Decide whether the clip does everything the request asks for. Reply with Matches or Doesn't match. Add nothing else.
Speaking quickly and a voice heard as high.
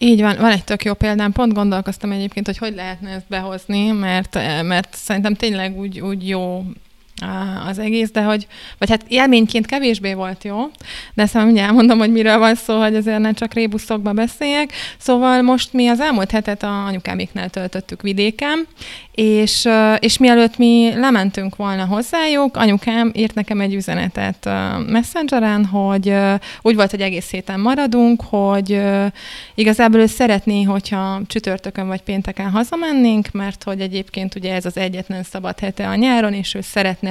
Matches